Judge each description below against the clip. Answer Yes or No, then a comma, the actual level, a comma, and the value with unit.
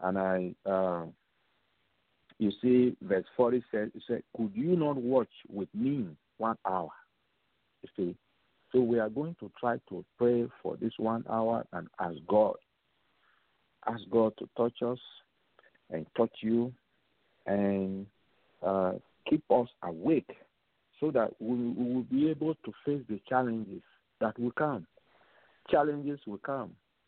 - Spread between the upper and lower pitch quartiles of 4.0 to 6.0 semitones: No, average, 3.3 semitones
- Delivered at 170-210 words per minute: No, average, 140 wpm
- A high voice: No, low, 115 Hz